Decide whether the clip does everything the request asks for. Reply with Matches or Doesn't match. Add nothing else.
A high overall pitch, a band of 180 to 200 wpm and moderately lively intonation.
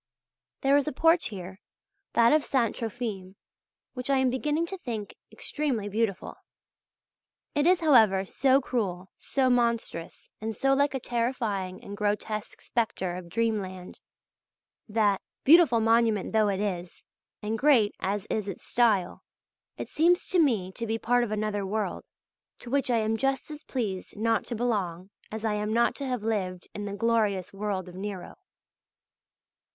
Doesn't match